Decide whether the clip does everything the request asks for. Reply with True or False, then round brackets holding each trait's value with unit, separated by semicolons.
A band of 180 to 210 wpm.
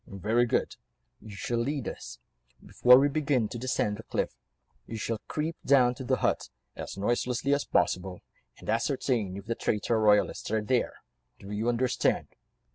False (165 wpm)